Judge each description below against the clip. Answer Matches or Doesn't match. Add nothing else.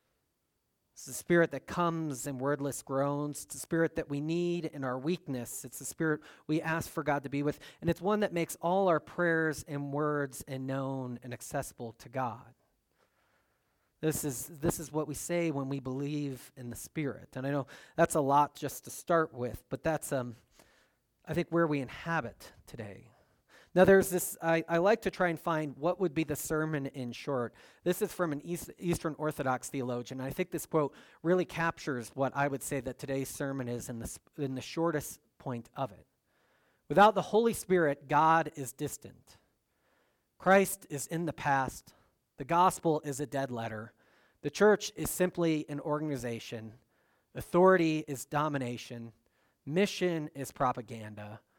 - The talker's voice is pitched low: Doesn't match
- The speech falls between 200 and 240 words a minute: Doesn't match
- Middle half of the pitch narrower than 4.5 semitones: Matches